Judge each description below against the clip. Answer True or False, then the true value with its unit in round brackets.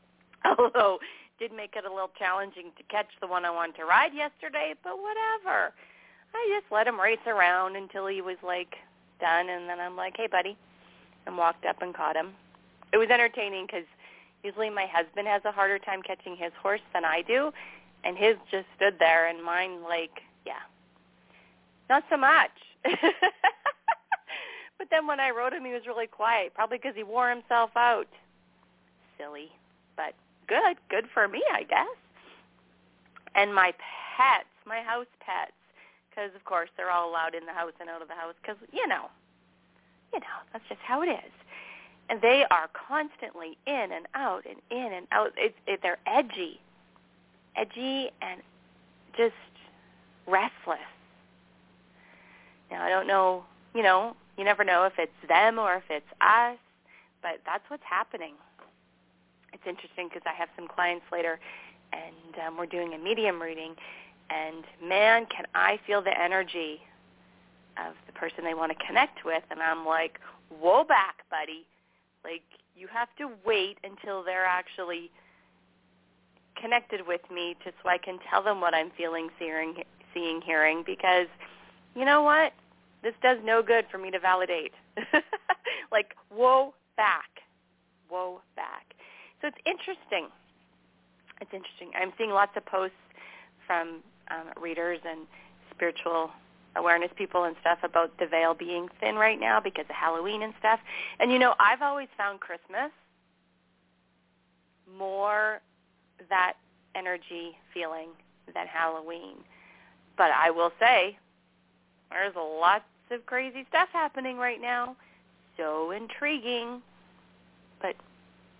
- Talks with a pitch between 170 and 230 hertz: True (190 Hz)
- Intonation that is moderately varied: False (5.7 semitones)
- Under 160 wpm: True (150 wpm)